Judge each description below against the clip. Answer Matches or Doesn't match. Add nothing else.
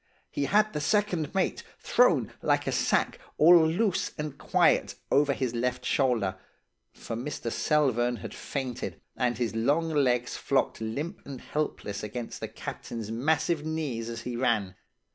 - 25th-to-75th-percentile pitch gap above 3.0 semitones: Matches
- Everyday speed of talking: Matches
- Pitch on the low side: Matches